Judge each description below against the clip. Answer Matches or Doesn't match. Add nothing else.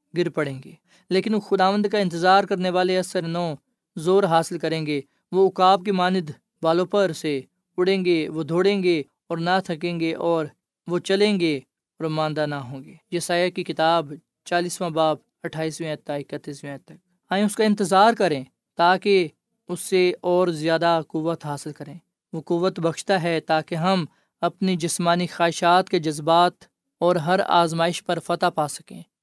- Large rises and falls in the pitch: Doesn't match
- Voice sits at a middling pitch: Matches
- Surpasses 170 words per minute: Doesn't match